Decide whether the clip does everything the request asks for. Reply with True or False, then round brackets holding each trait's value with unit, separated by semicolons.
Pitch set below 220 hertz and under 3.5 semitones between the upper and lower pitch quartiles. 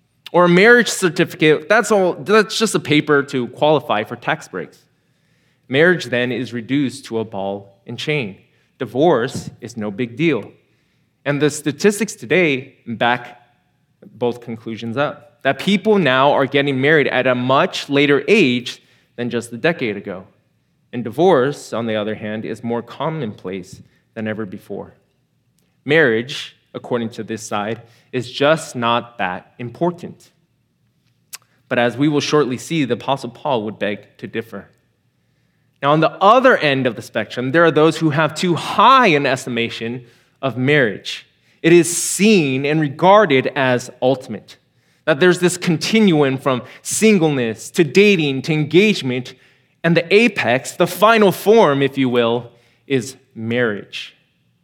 False (135 Hz; 5.3 semitones)